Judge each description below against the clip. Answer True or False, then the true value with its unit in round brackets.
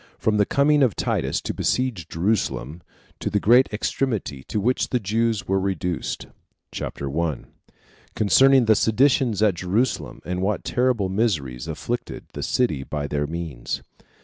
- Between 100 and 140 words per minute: False (150 wpm)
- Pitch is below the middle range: True (105 Hz)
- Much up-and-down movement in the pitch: True (5.9 semitones)